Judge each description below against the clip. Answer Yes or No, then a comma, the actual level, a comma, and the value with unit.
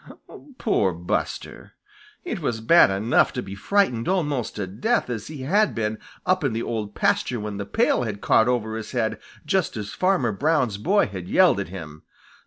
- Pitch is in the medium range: No, low, 115 Hz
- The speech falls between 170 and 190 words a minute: Yes, average, 185 wpm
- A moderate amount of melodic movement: No, wide, 7.4 semitones